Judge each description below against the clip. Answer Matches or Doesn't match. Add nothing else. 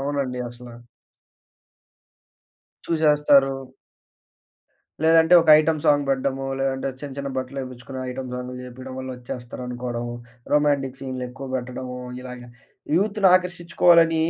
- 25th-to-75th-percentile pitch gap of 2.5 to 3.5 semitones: Matches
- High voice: Doesn't match